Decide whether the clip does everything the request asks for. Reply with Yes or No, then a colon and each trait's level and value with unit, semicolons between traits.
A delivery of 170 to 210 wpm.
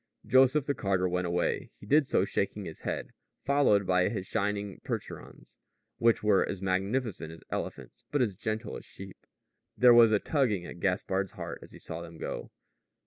Yes: average, 180 wpm